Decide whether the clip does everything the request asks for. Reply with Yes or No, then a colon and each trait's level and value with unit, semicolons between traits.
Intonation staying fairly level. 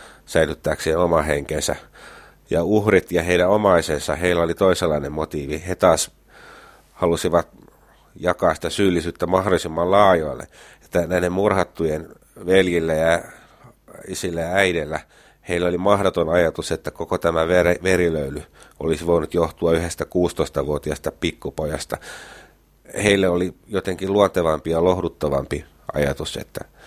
Yes: narrow, 2.3 semitones